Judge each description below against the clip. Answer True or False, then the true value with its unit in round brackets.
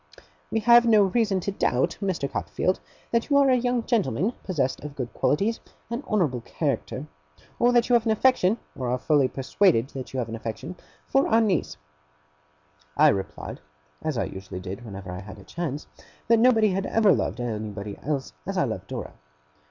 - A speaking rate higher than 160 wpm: True (185 wpm)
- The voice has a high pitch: False (175 Hz)